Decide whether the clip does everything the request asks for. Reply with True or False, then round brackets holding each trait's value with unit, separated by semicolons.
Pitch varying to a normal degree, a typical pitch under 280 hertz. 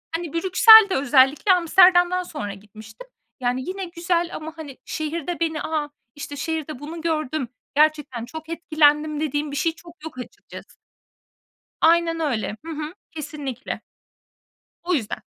False (3.0 semitones; 310 Hz)